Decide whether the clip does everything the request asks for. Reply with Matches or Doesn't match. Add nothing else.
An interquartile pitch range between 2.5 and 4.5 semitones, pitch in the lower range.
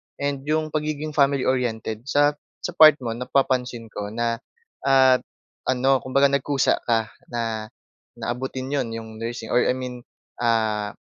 Matches